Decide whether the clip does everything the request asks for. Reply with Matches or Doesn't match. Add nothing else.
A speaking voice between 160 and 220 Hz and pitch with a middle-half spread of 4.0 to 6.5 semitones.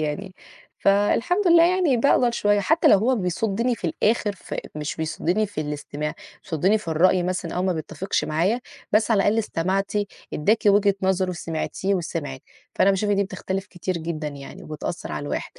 Matches